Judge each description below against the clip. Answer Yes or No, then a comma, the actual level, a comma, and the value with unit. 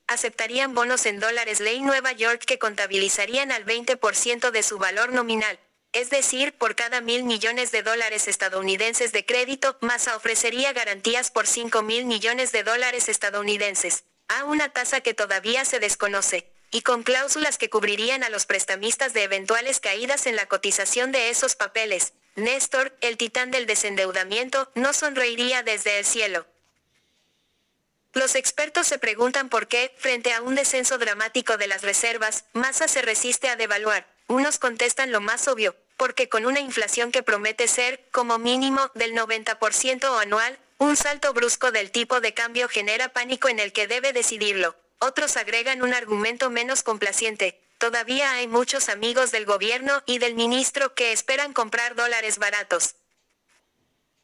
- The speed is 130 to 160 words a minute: Yes, average, 155 wpm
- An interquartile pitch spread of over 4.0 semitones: No, average, 3.2 semitones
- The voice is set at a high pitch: Yes, high, 235 Hz